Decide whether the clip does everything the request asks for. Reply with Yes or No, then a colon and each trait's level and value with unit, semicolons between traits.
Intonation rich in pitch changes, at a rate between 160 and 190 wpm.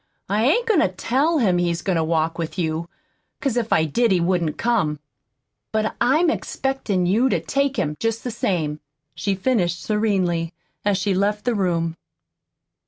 Yes: wide, 5.9 semitones; average, 170 wpm